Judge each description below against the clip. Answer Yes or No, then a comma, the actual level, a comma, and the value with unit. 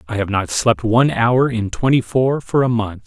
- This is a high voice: No, low, 115 Hz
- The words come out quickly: Yes, fast, 235 wpm